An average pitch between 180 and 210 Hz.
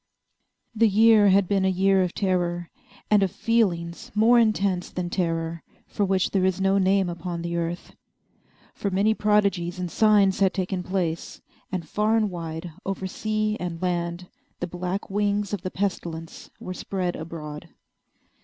Yes: medium, 185 Hz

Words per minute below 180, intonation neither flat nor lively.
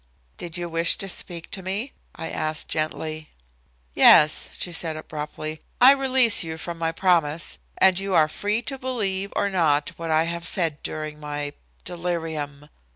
Yes: average, 160 wpm; average, 3.6 semitones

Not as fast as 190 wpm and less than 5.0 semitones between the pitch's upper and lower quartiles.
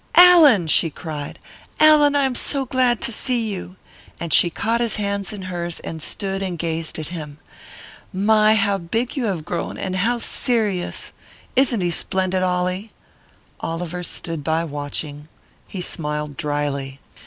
No: average, 155 wpm; wide, 5.4 semitones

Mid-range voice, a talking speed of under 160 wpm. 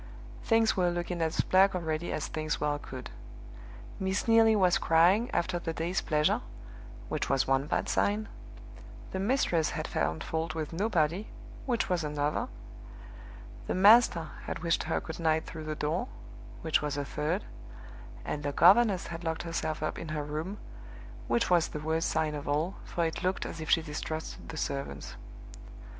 No: medium, 165 Hz; average, 170 wpm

